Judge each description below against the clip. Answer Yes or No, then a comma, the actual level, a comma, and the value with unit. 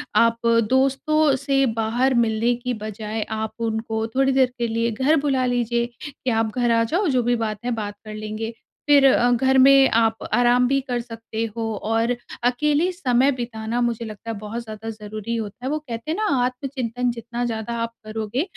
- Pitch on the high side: Yes, high, 235 Hz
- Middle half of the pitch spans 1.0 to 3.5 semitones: Yes, average, 2.8 semitones